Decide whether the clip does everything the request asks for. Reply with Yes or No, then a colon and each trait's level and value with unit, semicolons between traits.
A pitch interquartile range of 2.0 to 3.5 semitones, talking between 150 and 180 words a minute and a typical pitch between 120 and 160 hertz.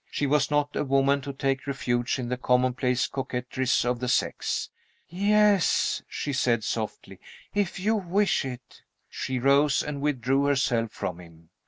Yes: average, 2.9 semitones; average, 155 wpm; low, 135 Hz